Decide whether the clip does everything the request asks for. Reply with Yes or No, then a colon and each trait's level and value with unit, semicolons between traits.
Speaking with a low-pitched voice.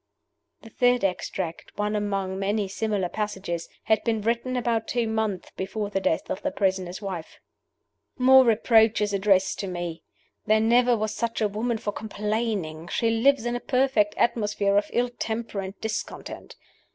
No: high, 210 Hz